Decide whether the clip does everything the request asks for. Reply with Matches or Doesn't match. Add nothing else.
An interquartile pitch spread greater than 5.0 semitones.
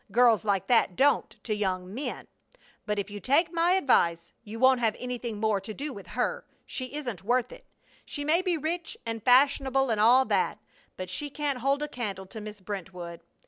Matches